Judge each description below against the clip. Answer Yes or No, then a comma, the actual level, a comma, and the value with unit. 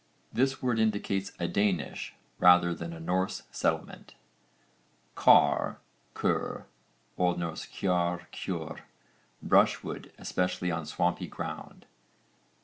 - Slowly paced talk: Yes, slow, 95 wpm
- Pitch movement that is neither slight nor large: No, narrow, 2.2 semitones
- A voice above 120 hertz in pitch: No, very low, 90 Hz